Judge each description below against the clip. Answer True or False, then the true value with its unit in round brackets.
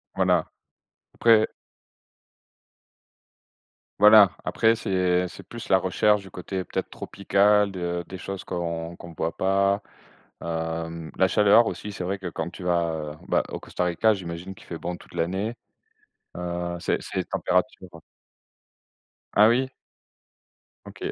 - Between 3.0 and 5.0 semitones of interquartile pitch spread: False (2.6 semitones)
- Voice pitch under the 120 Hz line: True (90 Hz)